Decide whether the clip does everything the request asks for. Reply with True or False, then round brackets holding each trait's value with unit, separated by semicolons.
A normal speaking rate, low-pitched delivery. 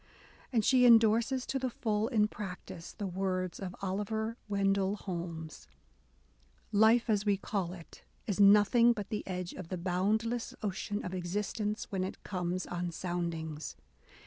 False (145 wpm; 200 Hz)